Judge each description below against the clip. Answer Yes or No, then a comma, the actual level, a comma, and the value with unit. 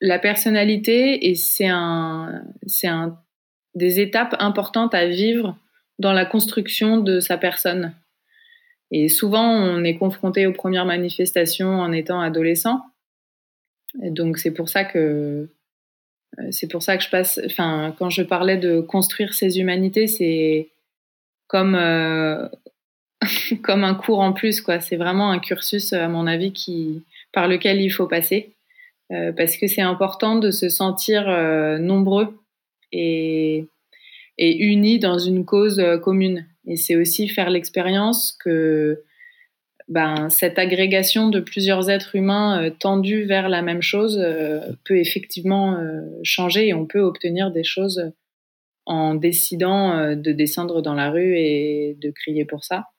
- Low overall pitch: No, medium, 185 Hz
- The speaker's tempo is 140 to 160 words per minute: Yes, average, 150 wpm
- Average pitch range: Yes, average, 3.3 semitones